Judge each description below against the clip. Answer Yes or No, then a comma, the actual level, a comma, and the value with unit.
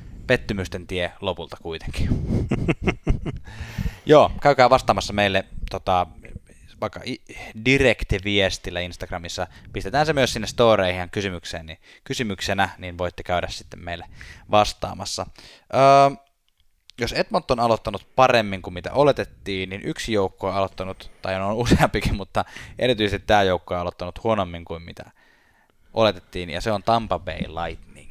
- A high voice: No, very low, 95 Hz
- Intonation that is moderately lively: Yes, average, 3.9 semitones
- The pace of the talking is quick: No, average, 130 wpm